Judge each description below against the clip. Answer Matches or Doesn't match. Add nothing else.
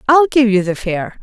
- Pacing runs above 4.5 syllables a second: Matches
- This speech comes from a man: Doesn't match